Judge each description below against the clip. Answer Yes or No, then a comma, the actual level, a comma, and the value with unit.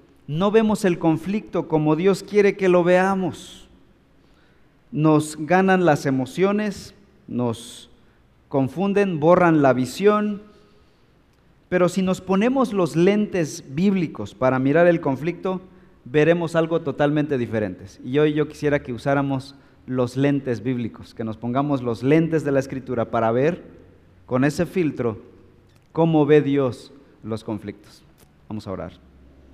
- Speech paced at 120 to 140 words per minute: Yes, average, 130 wpm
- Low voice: No, medium, 145 Hz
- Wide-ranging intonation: Yes, wide, 6.9 semitones